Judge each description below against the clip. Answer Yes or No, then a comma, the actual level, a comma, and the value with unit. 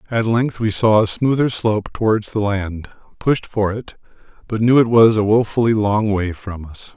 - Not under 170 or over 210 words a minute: Yes, average, 200 wpm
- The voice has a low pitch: Yes, low, 105 Hz